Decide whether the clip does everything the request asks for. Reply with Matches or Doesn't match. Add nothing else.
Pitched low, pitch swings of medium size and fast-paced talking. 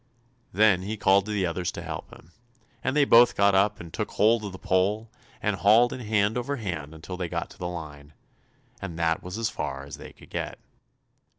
Matches